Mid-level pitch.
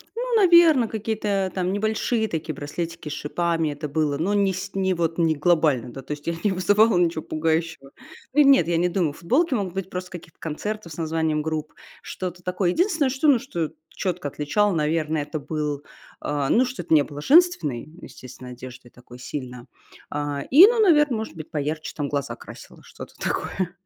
Yes: medium, 170 Hz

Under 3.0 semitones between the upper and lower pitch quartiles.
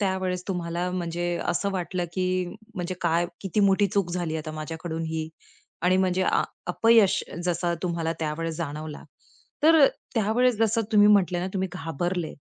Yes: narrow, 2.5 semitones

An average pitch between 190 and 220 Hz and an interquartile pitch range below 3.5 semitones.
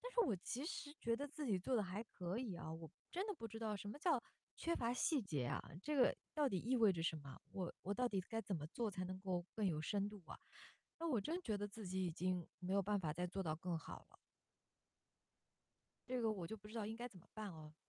No: high, 205 Hz; average, 5.2 semitones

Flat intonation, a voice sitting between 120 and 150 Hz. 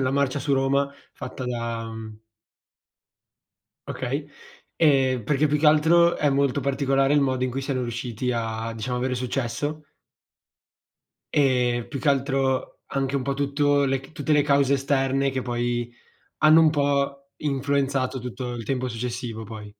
Yes: narrow, 2.3 semitones; low, 135 Hz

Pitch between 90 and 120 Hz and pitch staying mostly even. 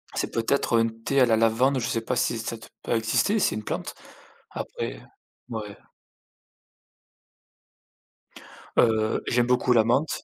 Yes: low, 115 Hz; narrow, 1.8 semitones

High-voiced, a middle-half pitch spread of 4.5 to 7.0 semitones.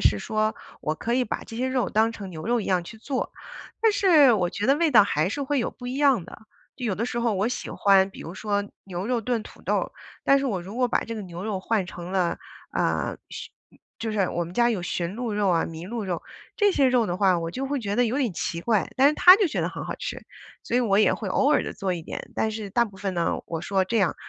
Yes: high, 215 Hz; average, 4.8 semitones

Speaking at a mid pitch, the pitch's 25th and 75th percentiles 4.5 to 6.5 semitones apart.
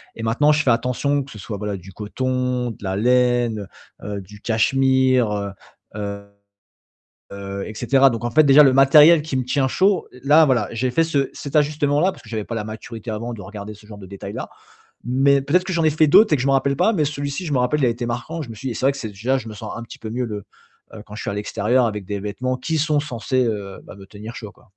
No: low, 125 Hz; average, 4.9 semitones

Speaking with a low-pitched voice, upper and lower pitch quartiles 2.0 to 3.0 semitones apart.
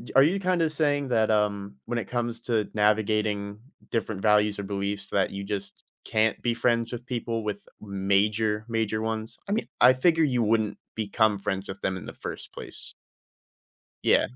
Yes: low, 110 Hz; average, 2.7 semitones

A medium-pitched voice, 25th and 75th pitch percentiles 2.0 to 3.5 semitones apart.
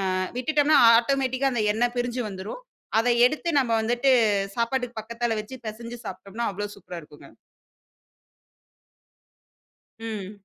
No: high, 235 Hz; average, 3.0 semitones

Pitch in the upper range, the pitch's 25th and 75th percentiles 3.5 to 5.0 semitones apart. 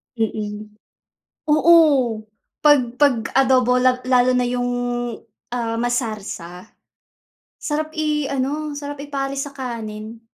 Yes: very high, 255 Hz; average, 3.9 semitones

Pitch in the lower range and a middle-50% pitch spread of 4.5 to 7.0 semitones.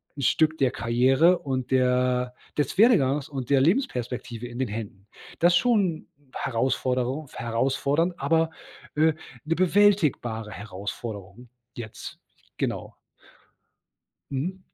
Yes: low, 130 Hz; average, 5.0 semitones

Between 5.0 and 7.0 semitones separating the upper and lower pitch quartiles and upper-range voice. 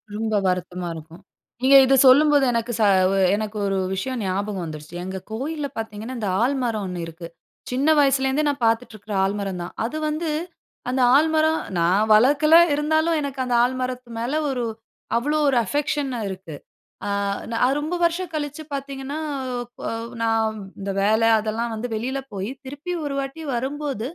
Yes: wide, 5.4 semitones; very high, 250 Hz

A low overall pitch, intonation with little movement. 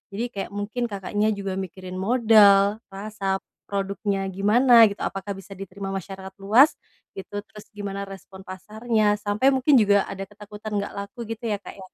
No: high, 205 Hz; narrow, 1.8 semitones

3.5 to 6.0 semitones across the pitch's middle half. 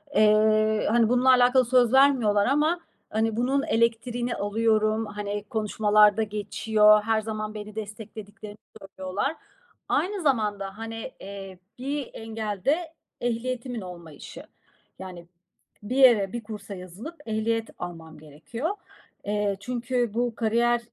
No: average, 2.7 semitones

